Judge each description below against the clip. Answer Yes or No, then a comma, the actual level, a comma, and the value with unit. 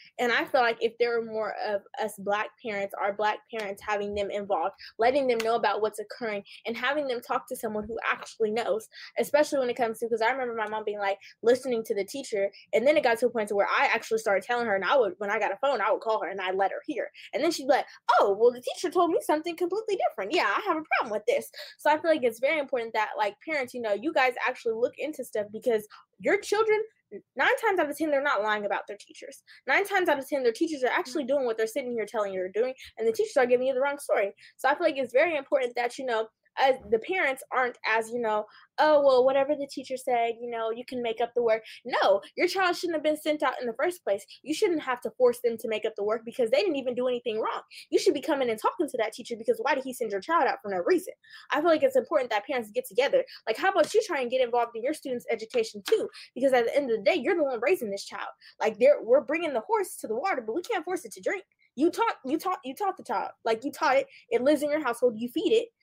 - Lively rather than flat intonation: Yes, wide, 6.4 semitones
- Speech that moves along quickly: Yes, fast, 285 wpm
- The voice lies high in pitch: Yes, very high, 260 Hz